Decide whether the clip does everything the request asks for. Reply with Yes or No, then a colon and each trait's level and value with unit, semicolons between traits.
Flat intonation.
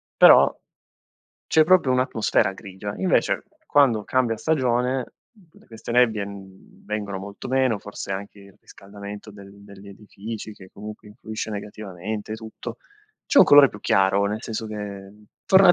No: average, 3.3 semitones